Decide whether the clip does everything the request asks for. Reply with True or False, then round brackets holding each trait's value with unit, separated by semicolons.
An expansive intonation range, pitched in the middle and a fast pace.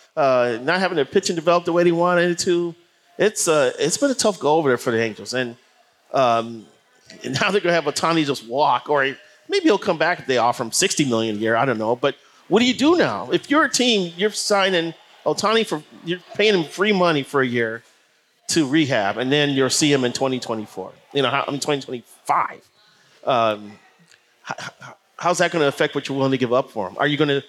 True (6.1 semitones; 150 Hz; 230 wpm)